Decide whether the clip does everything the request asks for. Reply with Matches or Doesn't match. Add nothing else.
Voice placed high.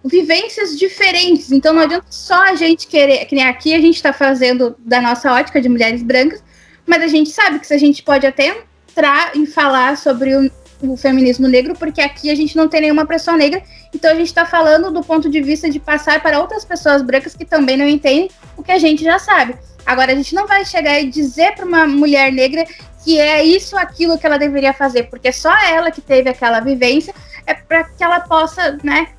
Matches